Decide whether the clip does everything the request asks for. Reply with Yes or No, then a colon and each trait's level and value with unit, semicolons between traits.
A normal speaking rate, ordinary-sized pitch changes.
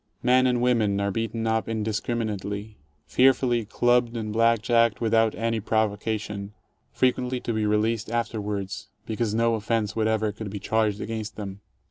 No: average, 145 wpm; narrow, 1.7 semitones